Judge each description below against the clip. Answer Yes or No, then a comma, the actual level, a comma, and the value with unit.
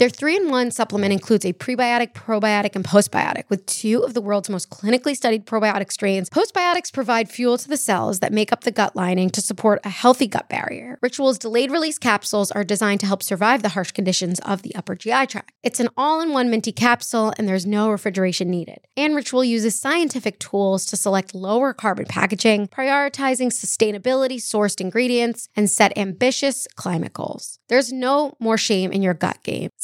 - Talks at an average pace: Yes, average, 185 wpm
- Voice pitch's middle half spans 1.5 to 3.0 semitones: No, average, 4.1 semitones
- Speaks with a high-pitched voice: Yes, high, 225 Hz